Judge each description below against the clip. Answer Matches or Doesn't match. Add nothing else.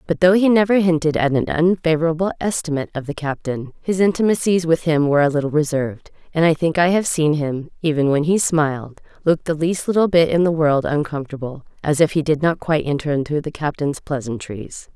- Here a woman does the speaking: Matches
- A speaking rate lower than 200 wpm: Doesn't match